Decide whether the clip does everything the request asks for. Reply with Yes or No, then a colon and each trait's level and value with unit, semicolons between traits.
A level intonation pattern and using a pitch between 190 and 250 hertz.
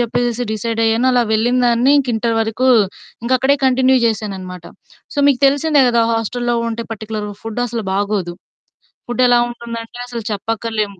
Yes: narrow, 2.1 semitones; high, 230 Hz